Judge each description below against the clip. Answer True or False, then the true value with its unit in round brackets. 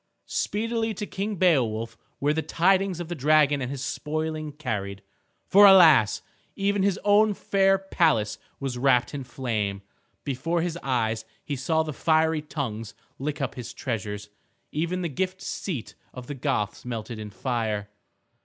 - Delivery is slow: False (155 wpm)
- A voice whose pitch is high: False (145 Hz)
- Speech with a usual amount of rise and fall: False (6.7 semitones)